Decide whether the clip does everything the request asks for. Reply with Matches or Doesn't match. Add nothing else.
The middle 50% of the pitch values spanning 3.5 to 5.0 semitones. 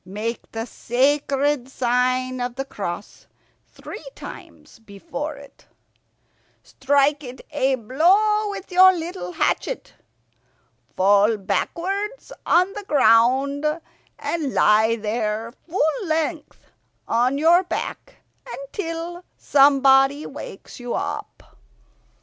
Doesn't match